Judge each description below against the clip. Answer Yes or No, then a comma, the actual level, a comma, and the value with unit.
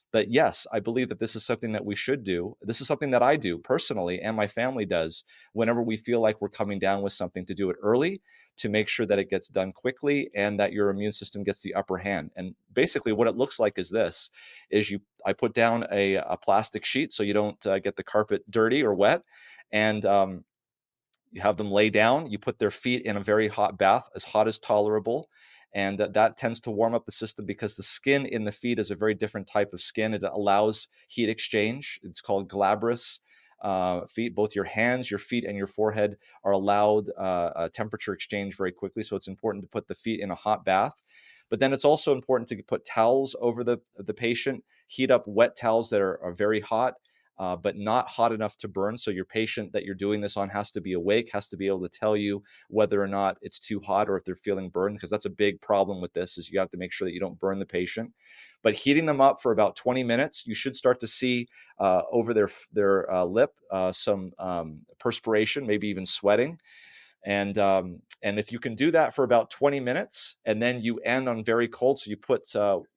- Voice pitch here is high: No, low, 105 Hz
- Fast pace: Yes, fast, 235 wpm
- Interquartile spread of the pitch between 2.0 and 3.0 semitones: Yes, average, 2.7 semitones